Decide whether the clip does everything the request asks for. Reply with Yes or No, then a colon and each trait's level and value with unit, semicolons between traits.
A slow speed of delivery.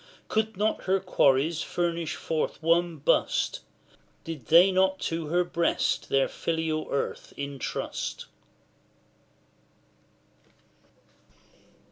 Yes: slow, 90 wpm